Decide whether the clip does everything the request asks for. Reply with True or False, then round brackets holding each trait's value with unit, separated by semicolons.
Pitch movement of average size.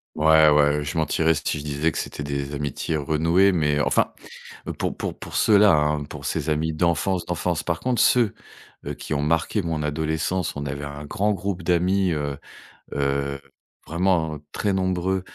True (3.5 semitones)